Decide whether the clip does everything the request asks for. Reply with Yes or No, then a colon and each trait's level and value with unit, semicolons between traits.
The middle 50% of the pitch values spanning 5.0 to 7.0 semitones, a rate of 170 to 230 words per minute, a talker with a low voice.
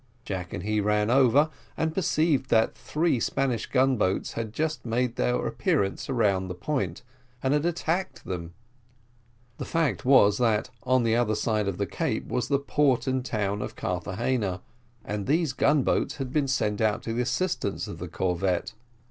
Yes: average, 5.3 semitones; average, 175 wpm; low, 115 Hz